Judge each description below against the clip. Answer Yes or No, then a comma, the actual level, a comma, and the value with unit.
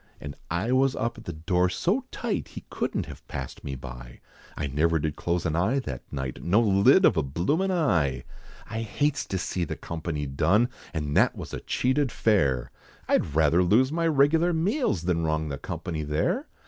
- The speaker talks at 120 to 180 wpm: No, average, 190 wpm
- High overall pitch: No, very low, 90 Hz